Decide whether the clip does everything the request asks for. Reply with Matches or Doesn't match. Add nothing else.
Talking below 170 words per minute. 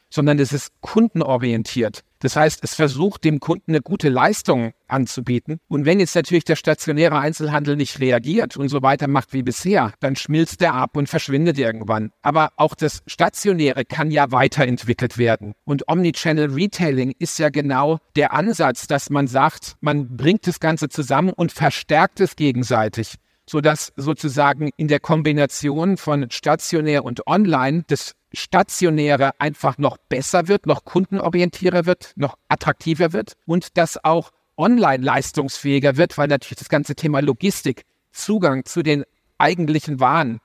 Matches